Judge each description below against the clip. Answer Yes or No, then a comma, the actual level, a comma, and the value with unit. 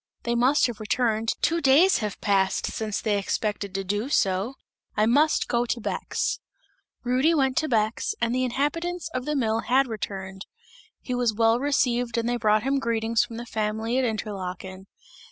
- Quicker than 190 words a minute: No, average, 175 wpm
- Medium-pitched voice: No, high, 235 Hz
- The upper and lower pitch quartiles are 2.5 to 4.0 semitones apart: Yes, average, 3.5 semitones